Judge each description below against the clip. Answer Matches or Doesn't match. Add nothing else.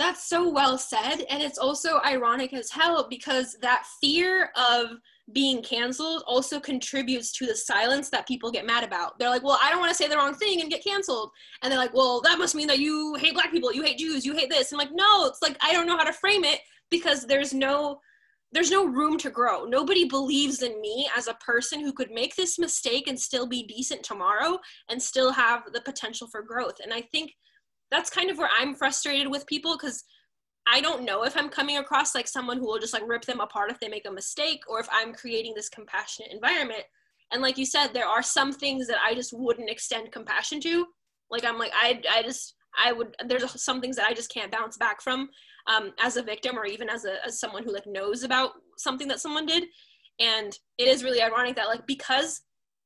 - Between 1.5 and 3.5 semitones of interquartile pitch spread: Doesn't match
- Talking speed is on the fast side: Matches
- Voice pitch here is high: Matches